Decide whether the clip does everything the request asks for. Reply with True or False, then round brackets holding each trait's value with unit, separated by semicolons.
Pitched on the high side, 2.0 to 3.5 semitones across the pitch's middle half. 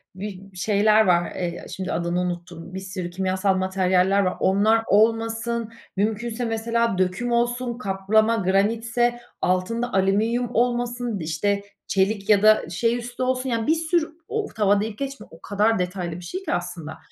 False (210 Hz; 3.9 semitones)